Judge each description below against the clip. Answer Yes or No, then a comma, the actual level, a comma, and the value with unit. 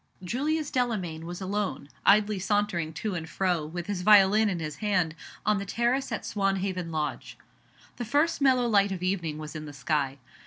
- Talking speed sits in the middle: Yes, average, 180 wpm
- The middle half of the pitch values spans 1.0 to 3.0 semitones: No, average, 4.4 semitones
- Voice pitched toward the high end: Yes, high, 195 Hz